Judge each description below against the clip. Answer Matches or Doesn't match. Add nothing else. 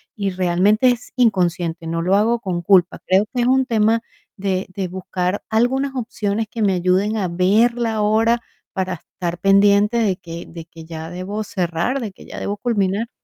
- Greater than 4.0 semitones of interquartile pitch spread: Doesn't match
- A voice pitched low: Doesn't match